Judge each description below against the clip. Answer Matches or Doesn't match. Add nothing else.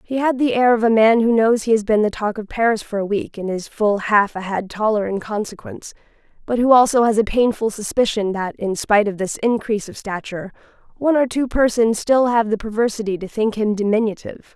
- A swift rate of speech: Matches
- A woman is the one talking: Matches